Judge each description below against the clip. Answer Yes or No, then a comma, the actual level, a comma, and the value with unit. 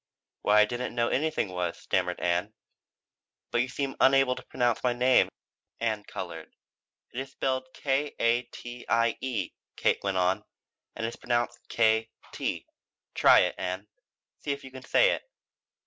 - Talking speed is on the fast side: No, average, 165 wpm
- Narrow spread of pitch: No, average, 3.6 semitones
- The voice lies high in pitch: No, low, 120 Hz